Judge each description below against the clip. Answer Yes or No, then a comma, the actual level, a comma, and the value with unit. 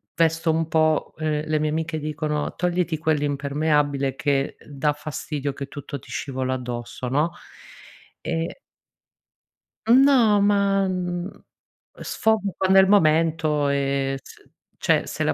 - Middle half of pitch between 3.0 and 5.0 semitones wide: Yes, average, 3.5 semitones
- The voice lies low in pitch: No, medium, 155 Hz